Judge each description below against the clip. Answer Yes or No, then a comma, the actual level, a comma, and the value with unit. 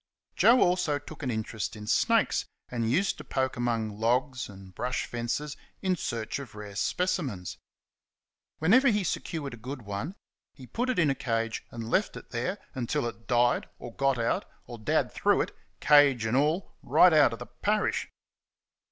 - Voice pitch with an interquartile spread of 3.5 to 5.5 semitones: Yes, average, 5.1 semitones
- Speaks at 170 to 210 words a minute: Yes, average, 175 wpm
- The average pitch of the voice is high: No, low, 125 Hz